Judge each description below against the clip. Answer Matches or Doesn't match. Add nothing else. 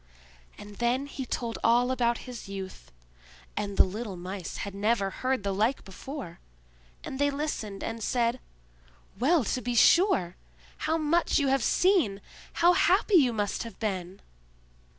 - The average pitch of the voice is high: Matches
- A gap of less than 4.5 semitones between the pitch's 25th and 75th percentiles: Doesn't match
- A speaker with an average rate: Matches